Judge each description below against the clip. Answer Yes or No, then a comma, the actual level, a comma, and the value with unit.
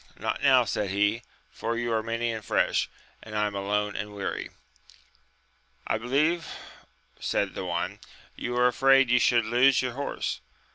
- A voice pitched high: No, low, 115 Hz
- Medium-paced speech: Yes, average, 170 wpm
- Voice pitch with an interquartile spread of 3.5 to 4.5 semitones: No, average, 2.9 semitones